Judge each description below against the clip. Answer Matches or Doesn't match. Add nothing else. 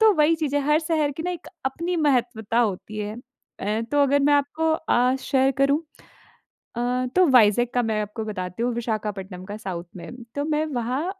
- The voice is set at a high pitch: Matches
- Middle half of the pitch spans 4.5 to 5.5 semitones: Matches